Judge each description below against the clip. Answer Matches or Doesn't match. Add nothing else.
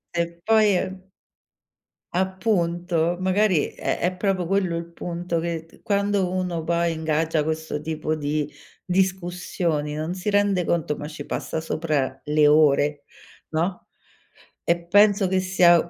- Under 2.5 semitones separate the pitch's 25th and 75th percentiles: Doesn't match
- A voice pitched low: Doesn't match